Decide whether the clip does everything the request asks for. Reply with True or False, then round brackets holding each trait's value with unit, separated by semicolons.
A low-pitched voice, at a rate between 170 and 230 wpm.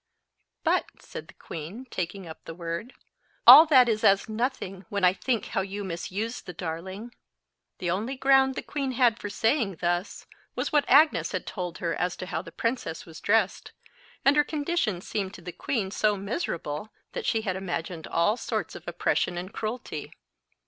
False (200 Hz; 180 wpm)